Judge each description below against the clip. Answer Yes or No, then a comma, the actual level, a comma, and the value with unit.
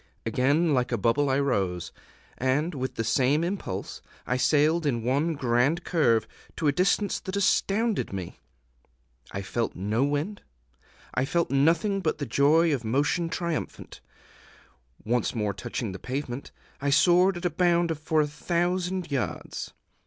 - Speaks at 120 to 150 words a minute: Yes, average, 145 wpm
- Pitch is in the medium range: Yes, medium, 145 Hz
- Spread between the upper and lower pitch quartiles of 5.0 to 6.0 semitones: Yes, wide, 5.4 semitones